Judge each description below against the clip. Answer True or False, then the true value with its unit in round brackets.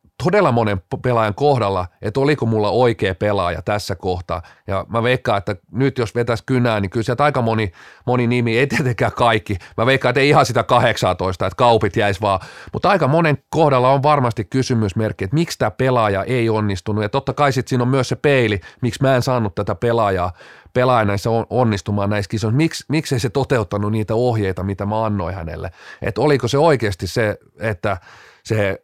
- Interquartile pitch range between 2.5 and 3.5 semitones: False (4.0 semitones)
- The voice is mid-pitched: False (115 Hz)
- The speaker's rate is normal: False (190 wpm)